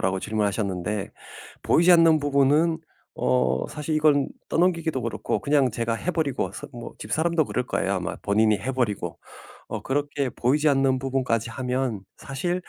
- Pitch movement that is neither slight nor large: No, wide, 5.9 semitones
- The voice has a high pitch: No, low, 130 Hz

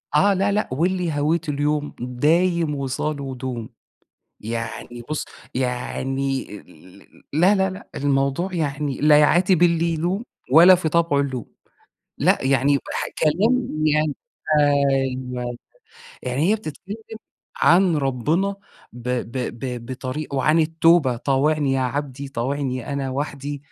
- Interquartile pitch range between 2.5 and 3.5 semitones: No, average, 4.1 semitones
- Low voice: No, medium, 145 Hz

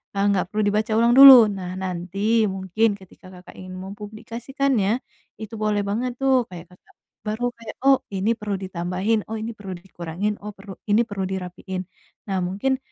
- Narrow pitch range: No, average, 3.2 semitones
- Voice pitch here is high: Yes, high, 205 Hz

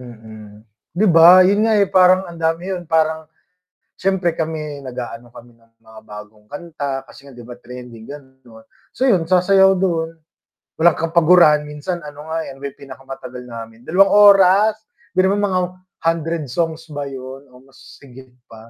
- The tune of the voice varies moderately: No, wide, 6.0 semitones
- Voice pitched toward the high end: No, medium, 150 Hz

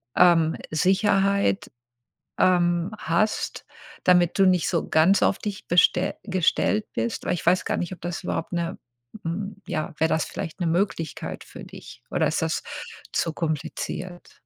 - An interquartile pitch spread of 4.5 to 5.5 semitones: No, narrow, 2.5 semitones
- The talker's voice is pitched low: No, medium, 175 Hz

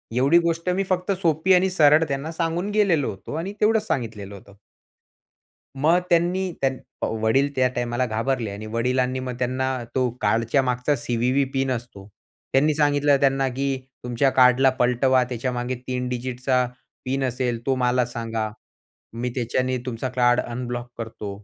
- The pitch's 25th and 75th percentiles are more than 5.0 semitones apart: No, average, 2.8 semitones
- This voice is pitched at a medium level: No, low, 130 Hz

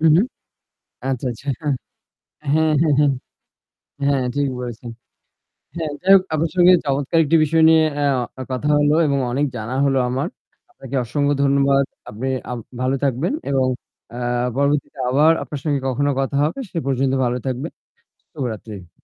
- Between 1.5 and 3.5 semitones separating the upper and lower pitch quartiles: Yes, average, 2.7 semitones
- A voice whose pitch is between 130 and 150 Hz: Yes, medium, 140 Hz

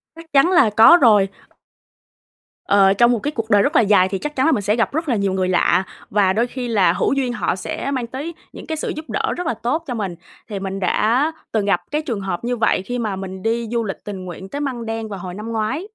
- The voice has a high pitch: Yes, high, 225 Hz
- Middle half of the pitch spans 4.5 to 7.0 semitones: Yes, average, 5.1 semitones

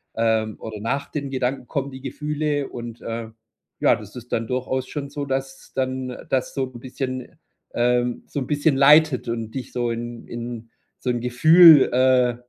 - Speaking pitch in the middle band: No, low, 130 Hz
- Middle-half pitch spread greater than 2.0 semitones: Yes, narrow, 2.6 semitones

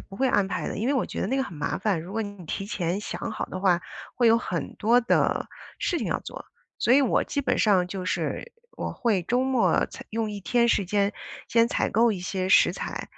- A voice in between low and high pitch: No, high, 210 Hz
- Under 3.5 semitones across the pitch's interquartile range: No, average, 3.9 semitones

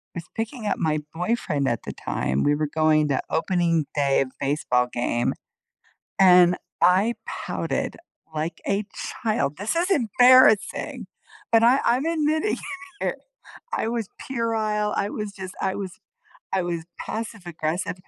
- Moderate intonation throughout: No, wide, 6.4 semitones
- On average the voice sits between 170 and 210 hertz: Yes, high, 190 Hz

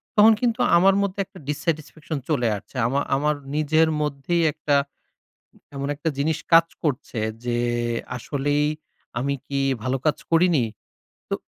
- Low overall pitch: No, medium, 150 Hz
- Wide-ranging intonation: No, average, 3.0 semitones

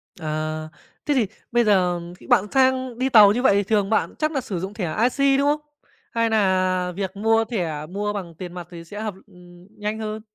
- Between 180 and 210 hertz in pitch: Yes, high, 205 Hz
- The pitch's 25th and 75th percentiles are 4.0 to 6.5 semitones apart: Yes, average, 4.3 semitones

